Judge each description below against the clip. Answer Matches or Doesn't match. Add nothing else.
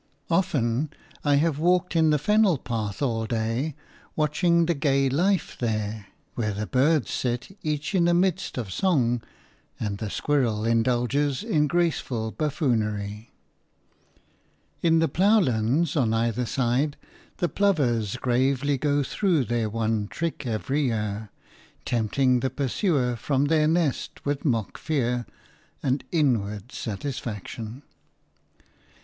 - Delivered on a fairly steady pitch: Doesn't match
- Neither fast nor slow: Doesn't match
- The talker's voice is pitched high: Doesn't match